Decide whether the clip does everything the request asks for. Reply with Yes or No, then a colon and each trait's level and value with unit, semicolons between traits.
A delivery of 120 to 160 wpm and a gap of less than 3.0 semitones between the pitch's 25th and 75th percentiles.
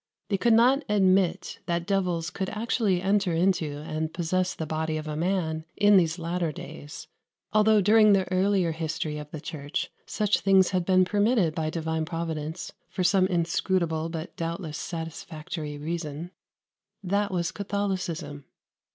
No: average, 150 wpm; average, 3.4 semitones